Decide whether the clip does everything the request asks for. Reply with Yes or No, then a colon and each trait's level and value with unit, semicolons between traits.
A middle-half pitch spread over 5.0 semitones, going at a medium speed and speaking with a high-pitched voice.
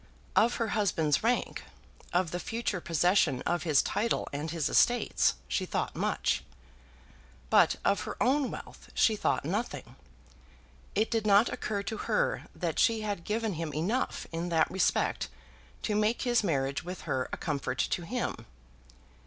Yes: wide, 5.4 semitones; average, 155 wpm; high, 200 Hz